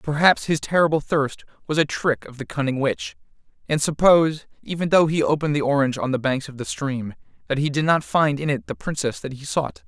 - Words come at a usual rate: No, fast, 225 wpm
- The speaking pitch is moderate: Yes, medium, 145 Hz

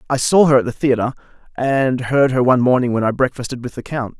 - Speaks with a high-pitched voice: No, low, 130 Hz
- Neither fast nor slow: No, fast, 245 wpm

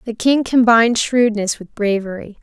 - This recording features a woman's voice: Yes, female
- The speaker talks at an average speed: Yes, average, 150 wpm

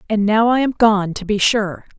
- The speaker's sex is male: No, female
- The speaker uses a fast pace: Yes, fast, 240 wpm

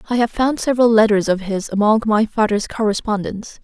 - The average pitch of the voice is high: Yes, high, 215 Hz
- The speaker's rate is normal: Yes, average, 180 wpm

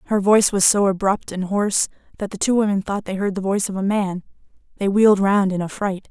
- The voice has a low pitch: No, high, 200 Hz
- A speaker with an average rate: No, fast, 235 wpm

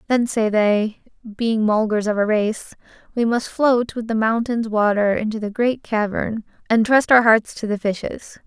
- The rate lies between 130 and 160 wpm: No, average, 185 wpm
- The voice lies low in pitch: No, high, 220 Hz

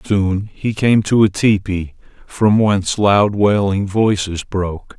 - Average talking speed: Yes, average, 145 wpm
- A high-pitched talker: No, low, 100 Hz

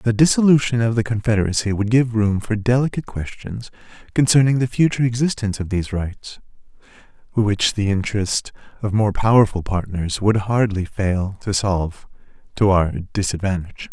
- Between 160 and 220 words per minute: No, average, 140 wpm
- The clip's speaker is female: No, male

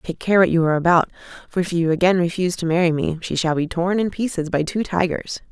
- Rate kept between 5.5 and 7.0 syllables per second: Yes, 6.3 syllables/s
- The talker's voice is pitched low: No, medium, 175 Hz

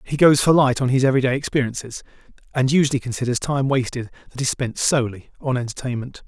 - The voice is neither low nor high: No, low, 130 Hz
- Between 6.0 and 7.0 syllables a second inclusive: Yes, 6.6 syllables/s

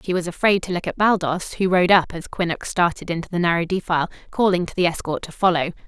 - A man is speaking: No, female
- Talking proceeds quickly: Yes, fast, 235 wpm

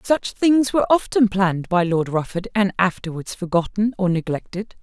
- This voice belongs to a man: No, female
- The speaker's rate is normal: Yes, average, 160 wpm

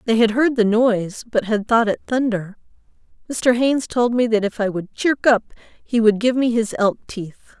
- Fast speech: Yes, fast, 215 wpm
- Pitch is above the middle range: Yes, high, 225 Hz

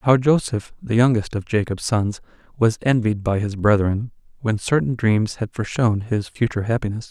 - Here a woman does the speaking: No, male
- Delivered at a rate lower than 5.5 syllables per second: Yes, 5.1 syllables/s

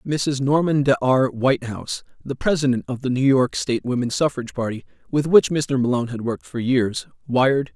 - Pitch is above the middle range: No, low, 130 Hz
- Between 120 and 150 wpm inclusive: No, average, 185 wpm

